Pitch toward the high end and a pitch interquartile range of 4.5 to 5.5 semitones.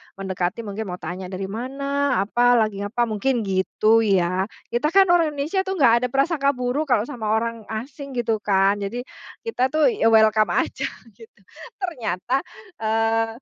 Yes: high, 225 Hz; average, 5.0 semitones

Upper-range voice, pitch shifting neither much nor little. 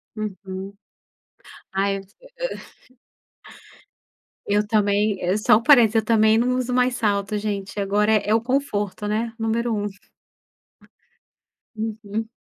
No: high, 215 Hz; narrow, 2.0 semitones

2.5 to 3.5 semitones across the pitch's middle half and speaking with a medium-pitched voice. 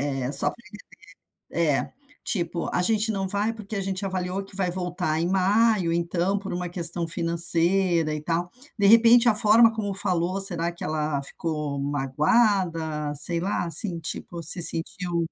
Yes: average, 3.0 semitones; medium, 175 Hz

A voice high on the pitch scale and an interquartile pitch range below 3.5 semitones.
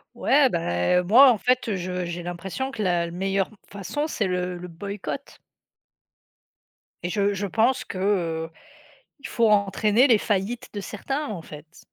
No: high, 195 Hz; average, 4.2 semitones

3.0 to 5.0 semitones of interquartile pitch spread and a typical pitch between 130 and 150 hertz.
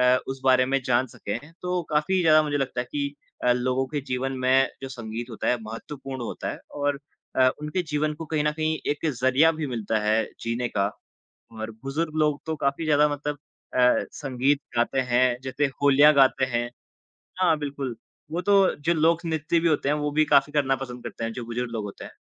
Yes: average, 3.4 semitones; low, 135 Hz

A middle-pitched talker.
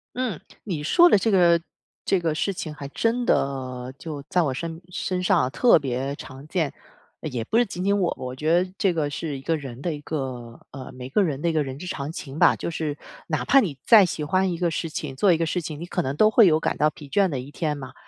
Yes: medium, 155 Hz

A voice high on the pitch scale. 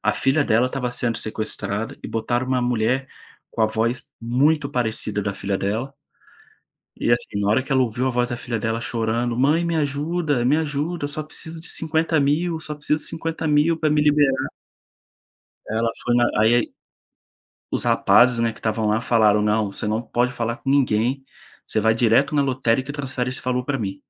No: low, 125 Hz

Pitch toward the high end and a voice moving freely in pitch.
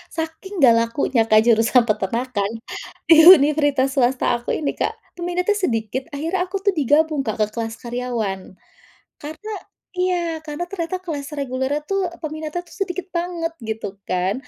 Yes: very high, 285 Hz; wide, 6.1 semitones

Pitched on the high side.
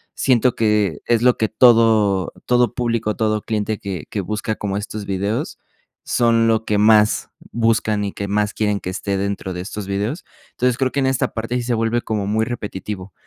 No: low, 110 Hz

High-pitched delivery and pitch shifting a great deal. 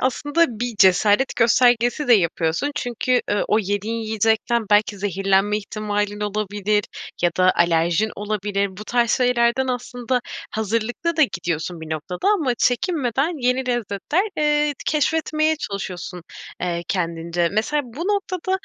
No: high, 220 Hz; average, 4.5 semitones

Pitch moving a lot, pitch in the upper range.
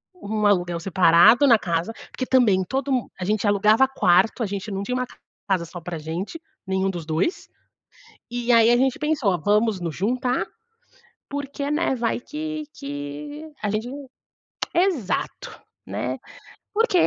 Yes: wide, 6.2 semitones; high, 215 Hz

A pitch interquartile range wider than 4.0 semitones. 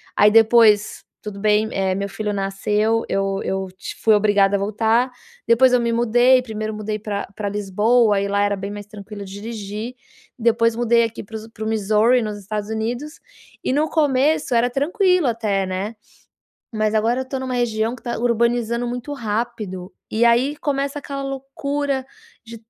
No: average, 2.9 semitones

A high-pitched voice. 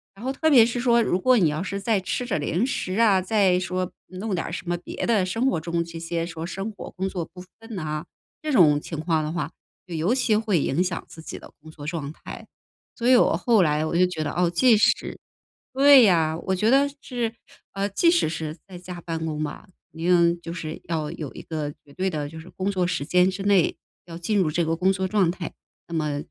No: medium, 180 Hz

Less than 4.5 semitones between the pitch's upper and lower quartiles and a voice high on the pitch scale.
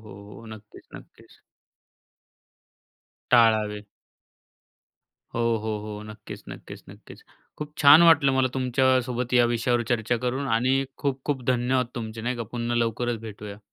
No: average, 2.7 semitones; low, 120 Hz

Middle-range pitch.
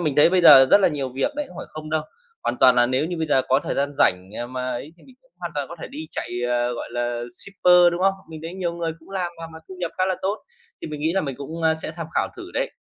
Yes: medium, 160 Hz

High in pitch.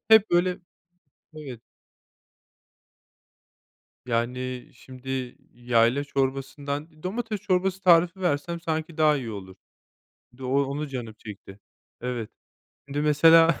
No: medium, 140 Hz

